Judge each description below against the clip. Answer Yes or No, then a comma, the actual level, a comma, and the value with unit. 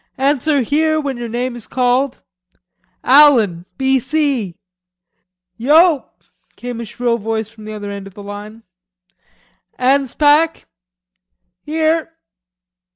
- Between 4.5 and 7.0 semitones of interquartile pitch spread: Yes, average, 4.8 semitones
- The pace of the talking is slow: Yes, slow, 100 wpm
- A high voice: Yes, very high, 255 Hz